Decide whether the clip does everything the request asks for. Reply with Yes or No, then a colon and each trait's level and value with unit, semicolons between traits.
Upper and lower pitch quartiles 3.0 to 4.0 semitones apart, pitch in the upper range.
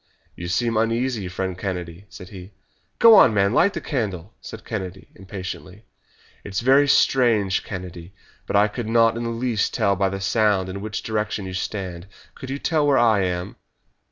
No: average, 3.7 semitones; low, 105 Hz